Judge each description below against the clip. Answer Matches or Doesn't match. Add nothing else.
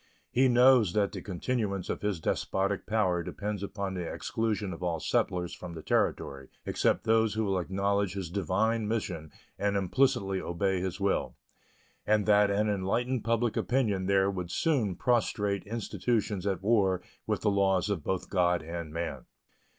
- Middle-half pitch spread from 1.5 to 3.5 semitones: Matches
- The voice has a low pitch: Matches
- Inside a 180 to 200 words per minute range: Doesn't match